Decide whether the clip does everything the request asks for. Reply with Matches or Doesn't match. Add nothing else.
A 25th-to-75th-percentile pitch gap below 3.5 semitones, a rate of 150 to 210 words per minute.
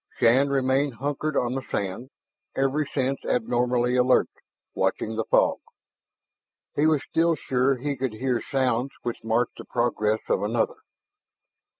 Doesn't match